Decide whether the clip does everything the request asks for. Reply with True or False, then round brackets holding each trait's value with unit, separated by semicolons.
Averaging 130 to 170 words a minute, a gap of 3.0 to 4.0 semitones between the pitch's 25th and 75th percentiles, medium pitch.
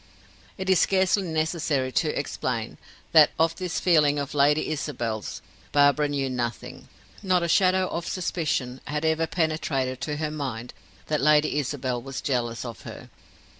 True (150 wpm; 3.7 semitones; 150 Hz)